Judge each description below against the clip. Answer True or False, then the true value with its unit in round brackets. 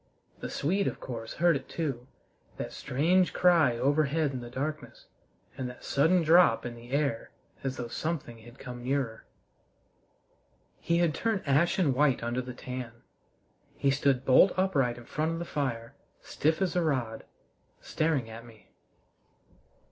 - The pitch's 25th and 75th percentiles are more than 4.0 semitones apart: True (4.8 semitones)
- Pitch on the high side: False (140 Hz)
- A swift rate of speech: False (155 wpm)